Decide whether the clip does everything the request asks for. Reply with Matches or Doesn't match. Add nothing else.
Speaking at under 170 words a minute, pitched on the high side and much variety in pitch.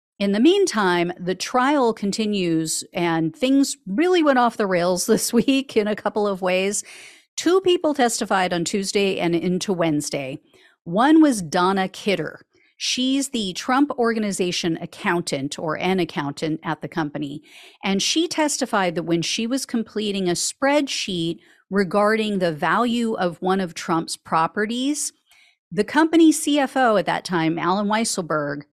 Matches